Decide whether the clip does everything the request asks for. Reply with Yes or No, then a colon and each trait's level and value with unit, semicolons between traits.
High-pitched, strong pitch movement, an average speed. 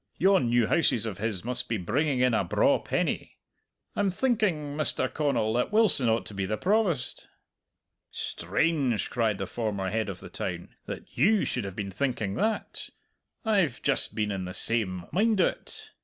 No: low, 120 Hz; wide, 8.2 semitones; average, 170 wpm